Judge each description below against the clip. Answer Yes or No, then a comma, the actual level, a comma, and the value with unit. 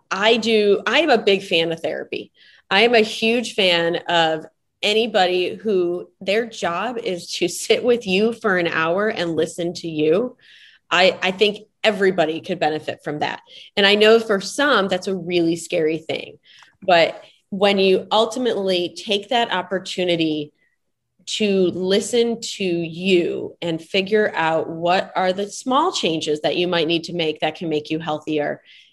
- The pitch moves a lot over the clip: No, average, 4.3 semitones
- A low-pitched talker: No, medium, 185 Hz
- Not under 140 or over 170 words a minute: Yes, average, 165 wpm